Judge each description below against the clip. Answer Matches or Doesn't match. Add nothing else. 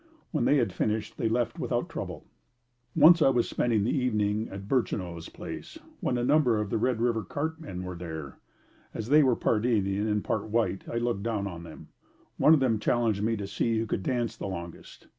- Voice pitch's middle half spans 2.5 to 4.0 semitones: Matches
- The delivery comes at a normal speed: Doesn't match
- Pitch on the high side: Doesn't match